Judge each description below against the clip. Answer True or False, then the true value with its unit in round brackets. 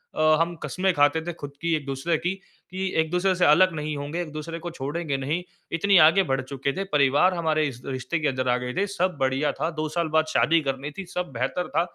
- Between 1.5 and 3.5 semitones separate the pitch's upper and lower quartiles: False (3.9 semitones)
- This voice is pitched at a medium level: True (155 Hz)